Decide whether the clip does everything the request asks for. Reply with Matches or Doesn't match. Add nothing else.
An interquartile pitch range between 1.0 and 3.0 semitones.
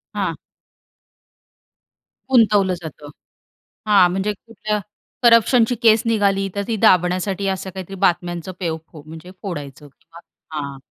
Doesn't match